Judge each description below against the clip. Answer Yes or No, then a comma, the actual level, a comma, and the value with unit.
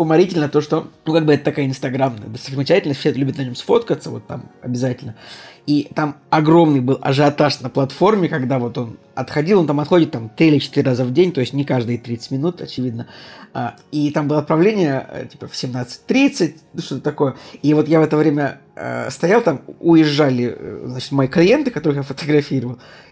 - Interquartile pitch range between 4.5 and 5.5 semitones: No, average, 3.2 semitones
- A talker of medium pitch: Yes, medium, 145 Hz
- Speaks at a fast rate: Yes, fast, 180 wpm